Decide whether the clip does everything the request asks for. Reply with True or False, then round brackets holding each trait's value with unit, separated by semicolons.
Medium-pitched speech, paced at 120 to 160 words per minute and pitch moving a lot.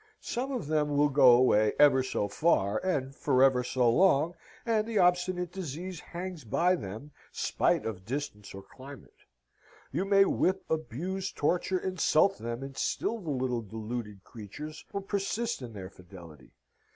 True (145 Hz; 150 wpm; 7.7 semitones)